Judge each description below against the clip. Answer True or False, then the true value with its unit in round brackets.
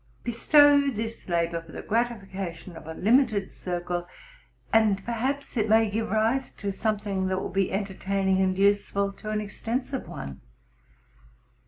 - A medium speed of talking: True (155 wpm)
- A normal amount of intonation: True (3.2 semitones)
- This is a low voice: False (205 Hz)